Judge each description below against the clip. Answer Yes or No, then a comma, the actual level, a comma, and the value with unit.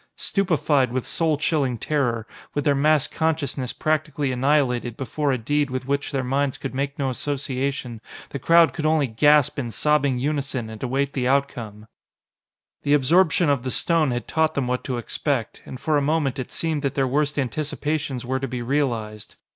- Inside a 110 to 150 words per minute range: No, average, 180 wpm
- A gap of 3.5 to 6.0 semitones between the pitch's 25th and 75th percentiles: No, average, 2.9 semitones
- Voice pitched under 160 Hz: Yes, medium, 140 Hz